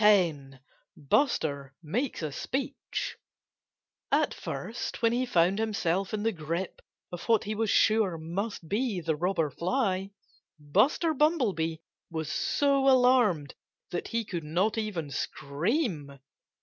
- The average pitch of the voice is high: Yes, high, 195 Hz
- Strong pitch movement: Yes, wide, 6.2 semitones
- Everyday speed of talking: No, slow, 125 wpm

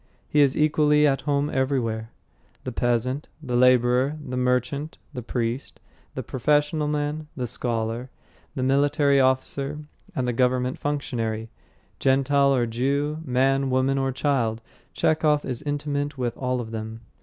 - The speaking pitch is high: No, low, 130 Hz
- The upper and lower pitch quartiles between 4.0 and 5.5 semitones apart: No, average, 2.8 semitones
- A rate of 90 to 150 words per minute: Yes, average, 140 wpm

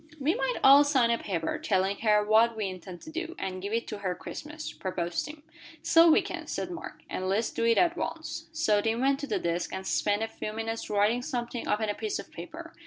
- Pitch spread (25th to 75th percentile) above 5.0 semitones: Yes, wide, 5.6 semitones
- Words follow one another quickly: Yes, fast, 235 wpm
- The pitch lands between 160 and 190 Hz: No, high, 225 Hz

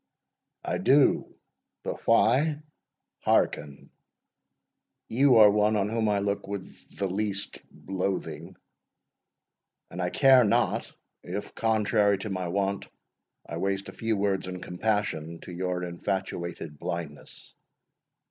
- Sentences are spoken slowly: Yes, slow, 120 wpm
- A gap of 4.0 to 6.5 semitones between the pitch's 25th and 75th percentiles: No, average, 3.0 semitones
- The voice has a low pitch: Yes, low, 100 Hz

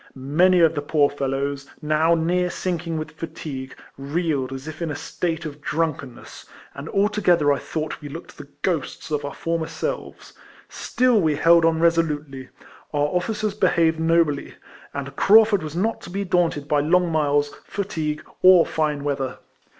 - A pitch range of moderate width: Yes, average, 3.2 semitones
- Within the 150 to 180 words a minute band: Yes, average, 165 wpm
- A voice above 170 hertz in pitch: No, medium, 160 Hz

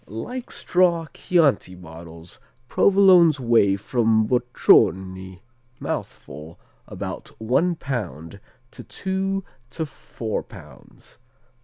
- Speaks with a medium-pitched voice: No, low, 120 Hz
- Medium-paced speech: No, slow, 90 wpm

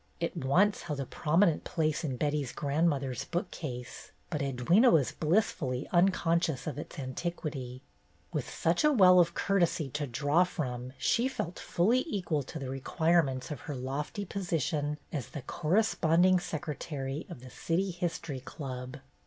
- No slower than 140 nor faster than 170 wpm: Yes, average, 145 wpm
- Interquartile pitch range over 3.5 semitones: Yes, average, 4.5 semitones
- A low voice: No, medium, 155 Hz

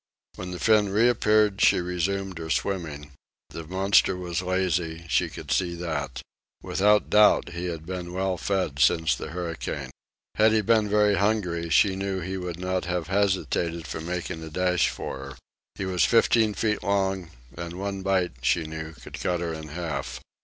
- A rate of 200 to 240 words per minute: No, average, 175 wpm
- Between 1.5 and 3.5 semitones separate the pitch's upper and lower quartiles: Yes, average, 2.8 semitones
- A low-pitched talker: Yes, very low, 90 Hz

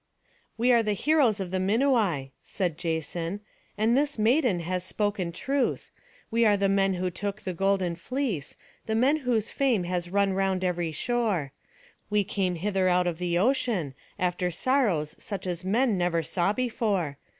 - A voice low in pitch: No, high, 195 Hz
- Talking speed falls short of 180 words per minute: Yes, average, 165 wpm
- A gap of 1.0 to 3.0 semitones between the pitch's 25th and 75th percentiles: No, average, 4.3 semitones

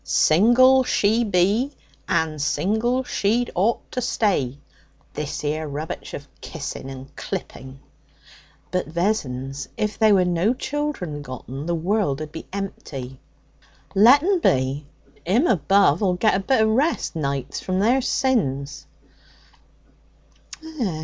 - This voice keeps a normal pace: No, slow, 120 wpm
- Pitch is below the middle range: No, medium, 180 Hz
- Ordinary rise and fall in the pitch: No, wide, 7.7 semitones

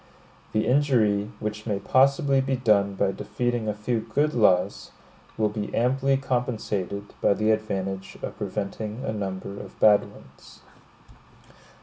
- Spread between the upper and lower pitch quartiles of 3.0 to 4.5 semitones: Yes, average, 3.6 semitones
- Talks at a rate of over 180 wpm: No, slow, 135 wpm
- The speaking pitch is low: Yes, low, 110 Hz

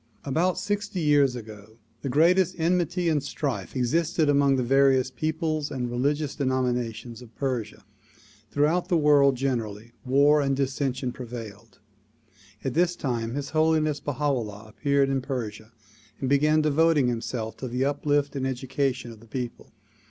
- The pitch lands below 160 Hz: Yes, low, 135 Hz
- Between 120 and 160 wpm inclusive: Yes, average, 145 wpm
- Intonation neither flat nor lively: Yes, average, 3.5 semitones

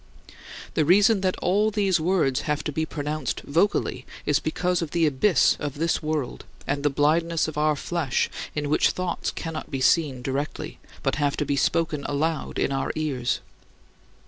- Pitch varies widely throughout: No, average, 2.9 semitones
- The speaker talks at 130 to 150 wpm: No, average, 175 wpm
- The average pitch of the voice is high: No, medium, 155 Hz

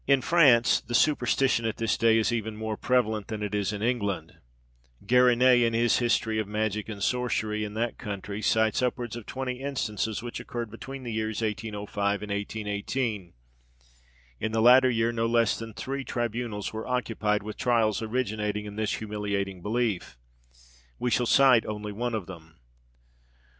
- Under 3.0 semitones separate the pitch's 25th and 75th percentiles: Yes, narrow, 2.5 semitones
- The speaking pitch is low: Yes, low, 110 Hz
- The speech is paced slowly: No, average, 165 wpm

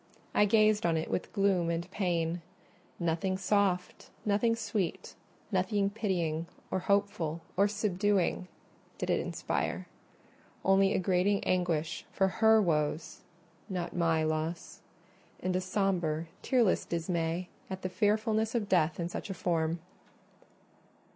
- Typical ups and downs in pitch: Yes, average, 3.3 semitones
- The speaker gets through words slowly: Yes, slow, 120 wpm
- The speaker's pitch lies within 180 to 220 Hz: Yes, medium, 185 Hz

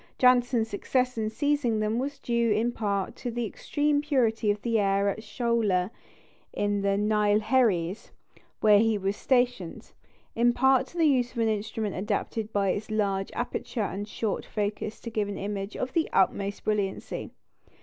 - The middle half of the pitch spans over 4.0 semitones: No, average, 3.0 semitones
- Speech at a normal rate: Yes, average, 165 wpm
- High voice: Yes, high, 220 Hz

